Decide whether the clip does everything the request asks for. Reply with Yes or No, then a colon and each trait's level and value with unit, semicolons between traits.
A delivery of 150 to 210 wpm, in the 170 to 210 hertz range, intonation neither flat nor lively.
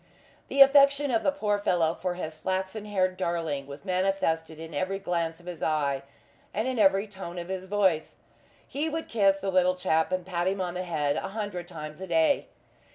Yes: average, 200 wpm; medium, 185 Hz; average, 3.4 semitones